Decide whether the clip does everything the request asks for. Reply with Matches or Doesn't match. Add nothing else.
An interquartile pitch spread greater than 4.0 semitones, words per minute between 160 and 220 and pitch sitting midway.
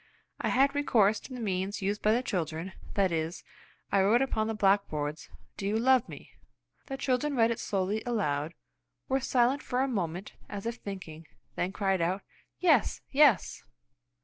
Doesn't match